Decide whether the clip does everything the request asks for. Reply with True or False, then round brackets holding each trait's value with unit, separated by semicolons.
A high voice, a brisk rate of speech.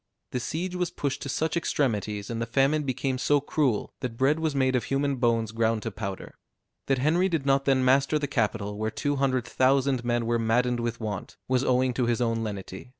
False (130 Hz; 210 wpm)